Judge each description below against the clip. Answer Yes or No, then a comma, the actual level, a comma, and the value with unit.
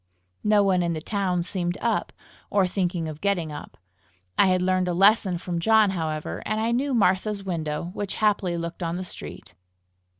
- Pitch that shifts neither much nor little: Yes, average, 3.0 semitones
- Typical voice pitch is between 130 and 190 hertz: Yes, medium, 185 Hz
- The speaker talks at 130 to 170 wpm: No, average, 180 wpm